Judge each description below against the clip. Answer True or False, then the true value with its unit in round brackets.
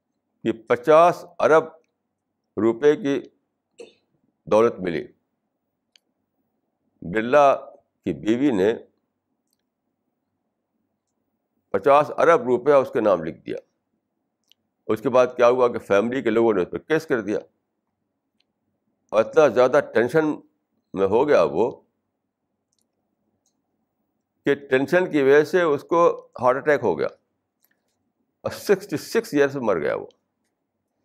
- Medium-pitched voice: True (150 Hz)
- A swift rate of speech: False (115 wpm)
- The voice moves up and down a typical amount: False (8.1 semitones)